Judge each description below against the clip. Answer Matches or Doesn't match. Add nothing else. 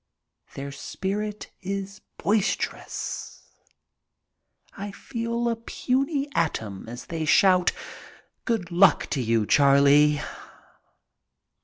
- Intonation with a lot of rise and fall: Matches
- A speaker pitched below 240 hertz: Matches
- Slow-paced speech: Matches